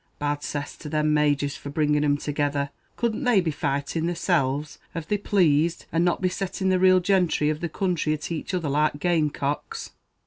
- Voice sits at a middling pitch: Yes, medium, 155 Hz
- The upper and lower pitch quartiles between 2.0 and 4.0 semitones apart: Yes, average, 3.5 semitones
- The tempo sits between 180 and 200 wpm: Yes, average, 195 wpm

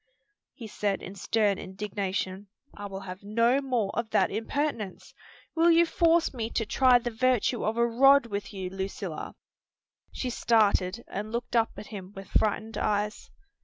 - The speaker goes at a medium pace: Yes, average, 165 wpm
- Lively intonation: No, average, 3.4 semitones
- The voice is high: Yes, high, 215 Hz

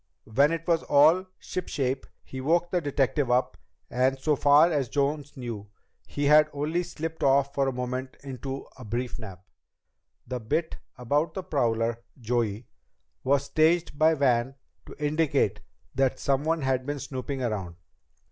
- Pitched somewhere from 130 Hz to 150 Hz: Yes, medium, 140 Hz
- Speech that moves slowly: No, average, 150 wpm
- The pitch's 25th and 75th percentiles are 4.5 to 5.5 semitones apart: No, average, 3.4 semitones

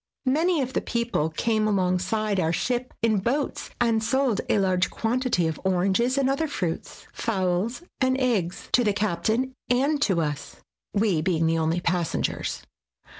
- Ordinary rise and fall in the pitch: No, wide, 5.9 semitones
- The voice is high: Yes, high, 215 Hz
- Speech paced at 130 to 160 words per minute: Yes, average, 155 wpm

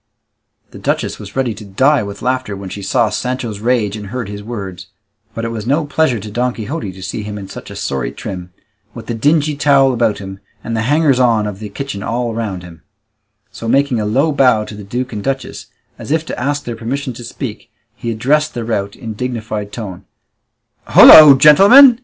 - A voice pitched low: Yes, low, 115 Hz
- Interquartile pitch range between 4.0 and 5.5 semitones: Yes, average, 4.4 semitones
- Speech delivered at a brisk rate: Yes, fast, 210 wpm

